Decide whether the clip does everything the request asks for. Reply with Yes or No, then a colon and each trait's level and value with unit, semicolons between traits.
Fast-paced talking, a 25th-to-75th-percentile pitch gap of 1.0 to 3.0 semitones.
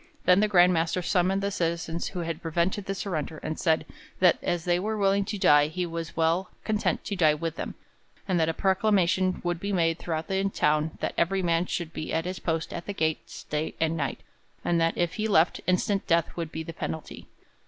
Yes: fast, 215 wpm; narrow, 2.6 semitones